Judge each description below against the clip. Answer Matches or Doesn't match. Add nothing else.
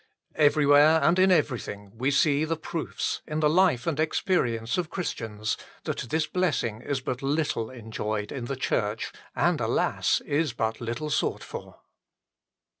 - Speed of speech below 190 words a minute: Matches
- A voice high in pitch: Doesn't match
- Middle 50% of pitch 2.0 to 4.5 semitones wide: Doesn't match